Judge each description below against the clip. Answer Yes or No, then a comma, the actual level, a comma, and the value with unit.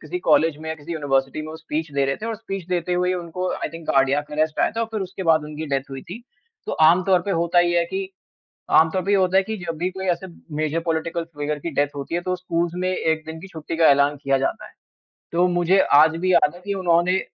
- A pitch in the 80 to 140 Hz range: No, medium, 165 Hz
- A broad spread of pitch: No, average, 3.1 semitones